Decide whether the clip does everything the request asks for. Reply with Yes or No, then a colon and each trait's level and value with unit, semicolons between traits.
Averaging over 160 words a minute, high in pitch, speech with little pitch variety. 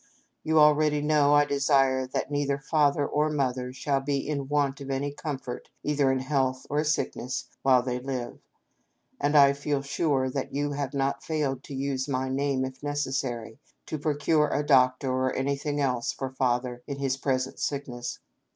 No: average, 170 wpm; medium, 140 Hz; narrow, 1.9 semitones